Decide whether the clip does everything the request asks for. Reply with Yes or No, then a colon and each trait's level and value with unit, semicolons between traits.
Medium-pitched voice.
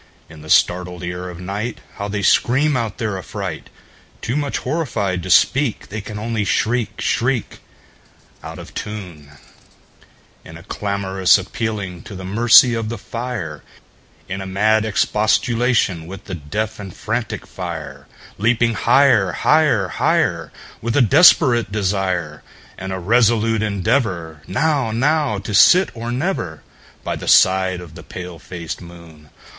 No: low, 105 Hz